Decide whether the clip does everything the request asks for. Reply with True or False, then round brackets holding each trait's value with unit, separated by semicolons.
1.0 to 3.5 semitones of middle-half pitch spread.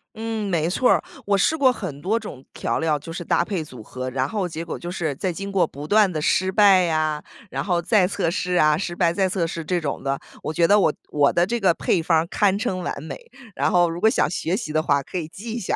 False (4.0 semitones)